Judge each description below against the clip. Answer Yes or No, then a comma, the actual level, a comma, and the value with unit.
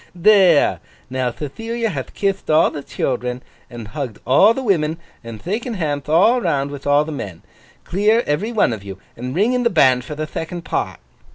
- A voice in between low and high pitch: Yes, medium, 155 Hz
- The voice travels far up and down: Yes, wide, 7.7 semitones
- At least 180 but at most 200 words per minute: Yes, average, 190 wpm